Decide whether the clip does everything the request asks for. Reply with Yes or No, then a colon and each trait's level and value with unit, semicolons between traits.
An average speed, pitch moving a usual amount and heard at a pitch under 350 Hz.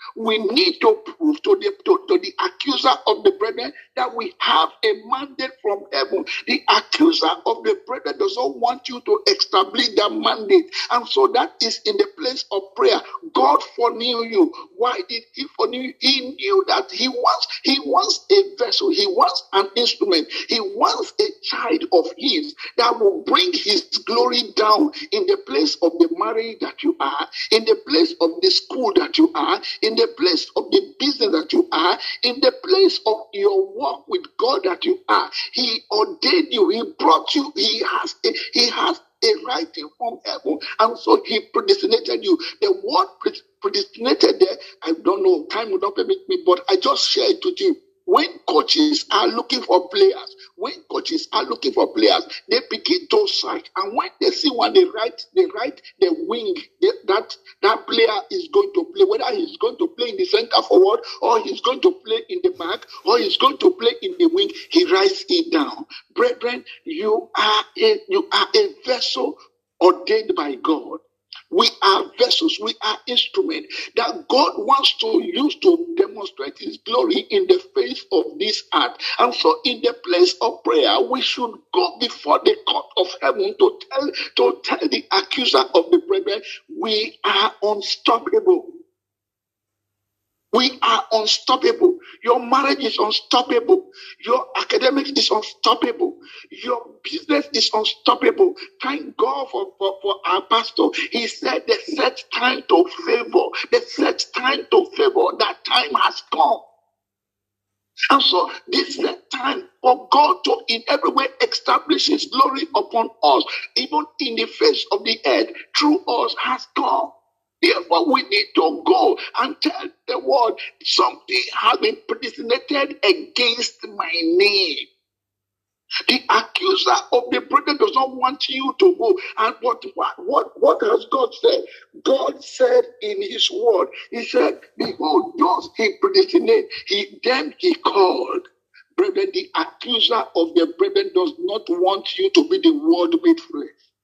No: average, 170 wpm; average, 4.3 semitones; very high, 370 Hz